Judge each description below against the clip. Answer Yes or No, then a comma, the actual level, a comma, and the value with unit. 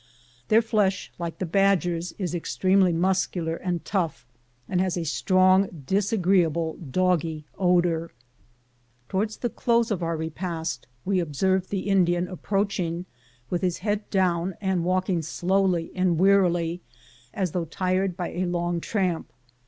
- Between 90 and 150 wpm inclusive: Yes, average, 140 wpm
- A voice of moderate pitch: Yes, medium, 180 Hz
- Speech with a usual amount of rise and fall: No, narrow, 2.2 semitones